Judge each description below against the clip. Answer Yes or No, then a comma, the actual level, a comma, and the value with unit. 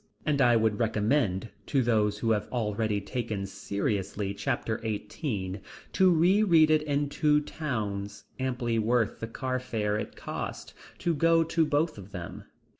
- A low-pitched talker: Yes, low, 115 Hz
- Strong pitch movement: Yes, wide, 6.2 semitones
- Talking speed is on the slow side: No, average, 150 wpm